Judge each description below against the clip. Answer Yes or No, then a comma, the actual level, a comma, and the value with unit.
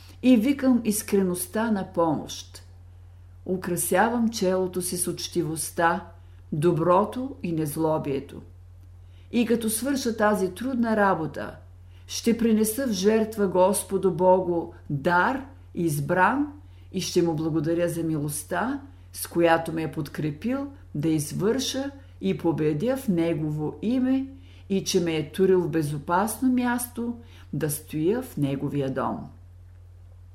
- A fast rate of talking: No, slow, 115 wpm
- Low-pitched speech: No, medium, 170 Hz